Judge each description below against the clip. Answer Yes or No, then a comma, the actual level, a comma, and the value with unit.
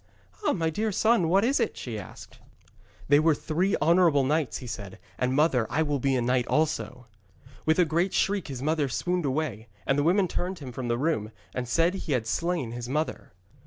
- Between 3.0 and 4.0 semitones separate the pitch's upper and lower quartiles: No, average, 5.3 semitones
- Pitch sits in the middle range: Yes, medium, 150 Hz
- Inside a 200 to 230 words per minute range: Yes, fast, 205 wpm